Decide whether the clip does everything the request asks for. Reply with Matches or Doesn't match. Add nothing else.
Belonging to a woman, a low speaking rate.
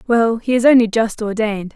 Doesn't match